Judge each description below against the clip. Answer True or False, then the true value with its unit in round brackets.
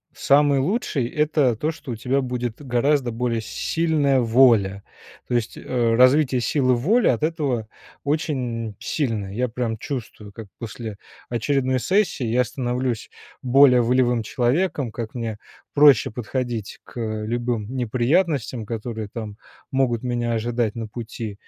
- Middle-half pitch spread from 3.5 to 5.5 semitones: False (3.0 semitones)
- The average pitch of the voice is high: False (125 Hz)